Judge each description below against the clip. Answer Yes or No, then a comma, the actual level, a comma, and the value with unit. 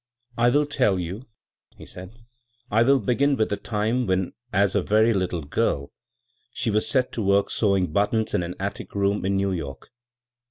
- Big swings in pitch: No, average, 3.8 semitones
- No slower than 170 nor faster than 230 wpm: Yes, average, 195 wpm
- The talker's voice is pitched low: Yes, low, 100 Hz